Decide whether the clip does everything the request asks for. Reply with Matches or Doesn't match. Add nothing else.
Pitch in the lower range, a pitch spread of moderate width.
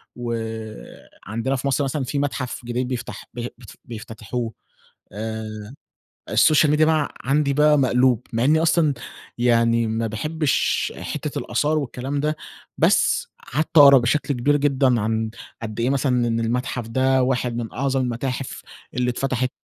Matches